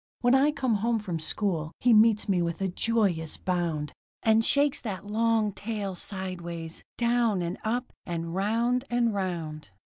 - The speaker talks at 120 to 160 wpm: Yes, average, 155 wpm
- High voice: Yes, high, 205 Hz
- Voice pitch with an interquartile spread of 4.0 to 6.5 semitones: Yes, average, 5.0 semitones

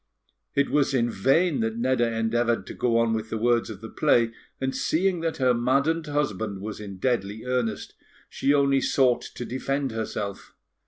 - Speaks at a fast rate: No, average, 175 wpm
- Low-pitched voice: Yes, low, 120 Hz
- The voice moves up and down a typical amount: Yes, average, 3.5 semitones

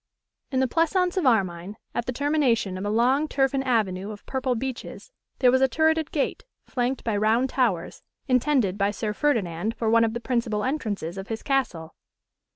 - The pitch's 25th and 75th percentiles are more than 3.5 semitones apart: Yes, average, 4.3 semitones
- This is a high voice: Yes, high, 240 Hz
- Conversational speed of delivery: Yes, average, 180 wpm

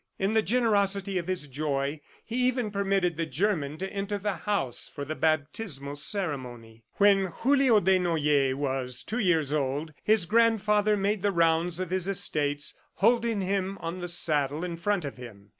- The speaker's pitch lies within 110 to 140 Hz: No, medium, 180 Hz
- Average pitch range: No, wide, 5.8 semitones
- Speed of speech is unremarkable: Yes, average, 165 wpm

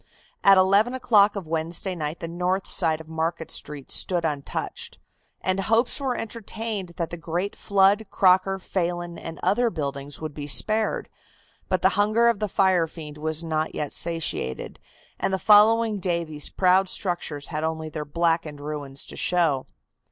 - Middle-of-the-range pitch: Yes, medium, 175 Hz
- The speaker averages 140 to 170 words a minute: Yes, average, 165 wpm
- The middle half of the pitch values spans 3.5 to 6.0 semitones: Yes, average, 4.1 semitones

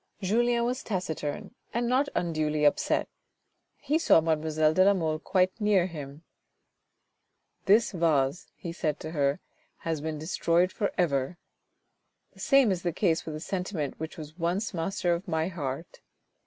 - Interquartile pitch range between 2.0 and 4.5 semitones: Yes, average, 3.7 semitones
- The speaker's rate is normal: Yes, average, 155 wpm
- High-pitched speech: No, medium, 170 Hz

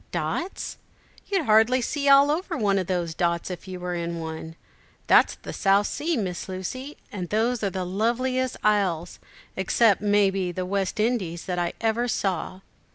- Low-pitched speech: No, high, 200 Hz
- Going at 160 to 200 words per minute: Yes, average, 170 wpm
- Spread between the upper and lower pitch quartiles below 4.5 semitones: No, average, 5.1 semitones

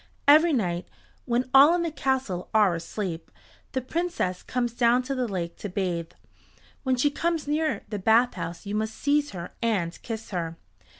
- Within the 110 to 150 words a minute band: No, average, 170 wpm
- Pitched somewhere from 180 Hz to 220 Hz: No, high, 230 Hz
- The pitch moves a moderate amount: No, wide, 7.1 semitones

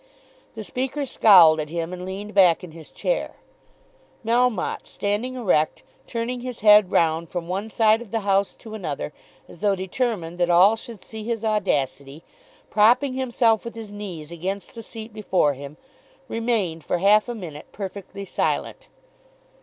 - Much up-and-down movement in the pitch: No, average, 4.6 semitones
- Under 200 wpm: Yes, average, 160 wpm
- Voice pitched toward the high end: Yes, high, 205 Hz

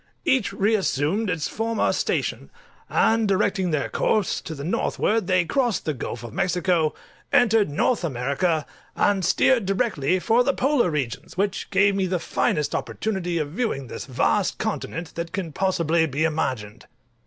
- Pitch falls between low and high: Yes, medium, 180 Hz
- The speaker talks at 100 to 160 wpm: Yes, average, 155 wpm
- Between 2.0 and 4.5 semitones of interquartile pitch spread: No, wide, 5.4 semitones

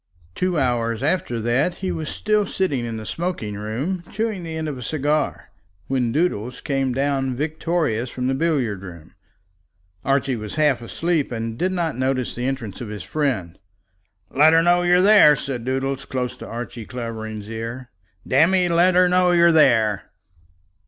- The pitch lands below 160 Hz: Yes, low, 135 Hz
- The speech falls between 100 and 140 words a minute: No, average, 170 wpm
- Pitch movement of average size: No, wide, 6.1 semitones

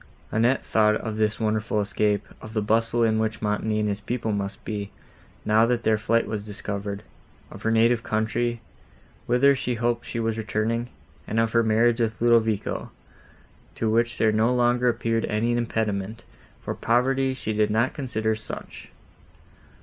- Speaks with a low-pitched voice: Yes, low, 110 Hz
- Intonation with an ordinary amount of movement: No, narrow, 1.6 semitones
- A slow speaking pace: No, average, 165 wpm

